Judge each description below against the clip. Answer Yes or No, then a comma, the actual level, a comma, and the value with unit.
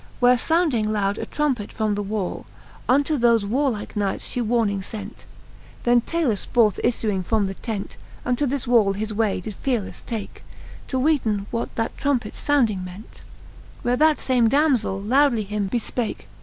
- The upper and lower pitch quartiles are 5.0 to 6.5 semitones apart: No, average, 3.7 semitones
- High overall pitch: Yes, high, 230 Hz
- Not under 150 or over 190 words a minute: Yes, average, 160 wpm